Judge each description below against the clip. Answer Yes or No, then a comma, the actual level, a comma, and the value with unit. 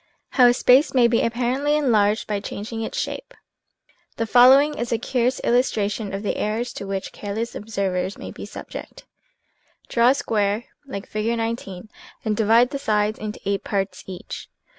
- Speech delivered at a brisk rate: No, average, 170 wpm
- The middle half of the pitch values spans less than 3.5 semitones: Yes, average, 3.0 semitones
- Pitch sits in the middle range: No, high, 225 Hz